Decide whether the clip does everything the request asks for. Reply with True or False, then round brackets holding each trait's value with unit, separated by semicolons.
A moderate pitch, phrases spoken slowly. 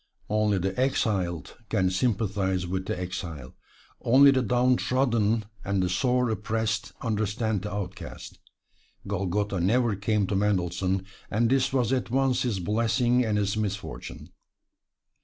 False (105 Hz; 130 wpm)